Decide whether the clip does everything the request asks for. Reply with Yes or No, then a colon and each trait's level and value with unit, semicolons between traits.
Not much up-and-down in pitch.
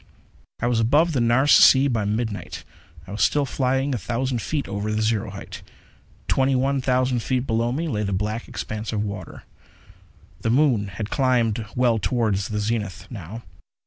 No: average, 3.6 semitones